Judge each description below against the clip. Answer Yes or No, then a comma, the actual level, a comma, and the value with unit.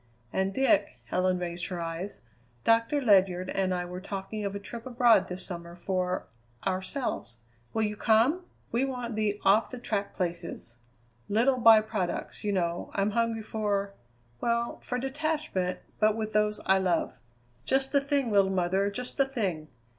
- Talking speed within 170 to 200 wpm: No, average, 160 wpm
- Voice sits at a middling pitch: No, high, 205 Hz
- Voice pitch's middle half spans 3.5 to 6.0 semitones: Yes, average, 4.2 semitones